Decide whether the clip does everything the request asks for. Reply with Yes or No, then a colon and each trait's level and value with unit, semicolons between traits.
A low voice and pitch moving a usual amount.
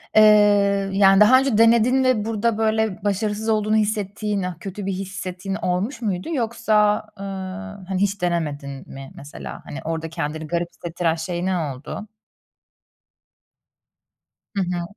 No: high, 195 Hz; average, 3.3 semitones